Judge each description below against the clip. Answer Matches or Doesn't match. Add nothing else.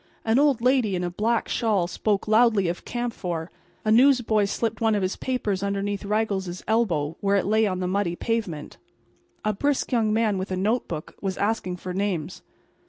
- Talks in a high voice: Matches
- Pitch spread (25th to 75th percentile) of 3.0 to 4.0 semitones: Matches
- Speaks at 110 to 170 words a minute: Doesn't match